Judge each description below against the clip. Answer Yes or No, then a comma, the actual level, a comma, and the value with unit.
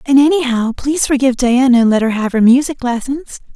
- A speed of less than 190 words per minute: No, fast, 205 wpm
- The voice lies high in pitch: Yes, very high, 255 Hz